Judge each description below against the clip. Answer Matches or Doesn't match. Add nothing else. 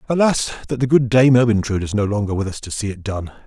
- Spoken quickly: Matches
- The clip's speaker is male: Matches